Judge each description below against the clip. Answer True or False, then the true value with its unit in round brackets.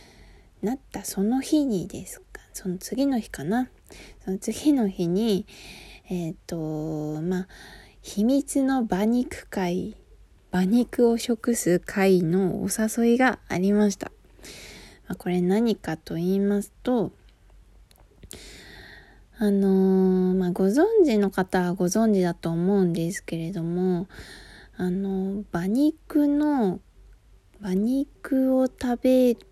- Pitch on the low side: False (200 Hz)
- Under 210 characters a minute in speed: True (200 characters per minute)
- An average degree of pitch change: True (4.7 semitones)